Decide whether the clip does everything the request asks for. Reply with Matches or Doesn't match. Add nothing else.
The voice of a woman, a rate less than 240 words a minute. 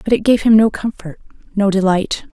Matches